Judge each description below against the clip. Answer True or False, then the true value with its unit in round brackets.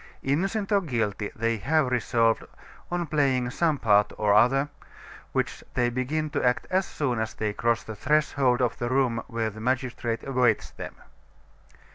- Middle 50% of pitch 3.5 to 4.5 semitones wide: True (3.9 semitones)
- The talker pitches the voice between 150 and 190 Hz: False (125 Hz)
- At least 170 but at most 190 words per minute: False (160 wpm)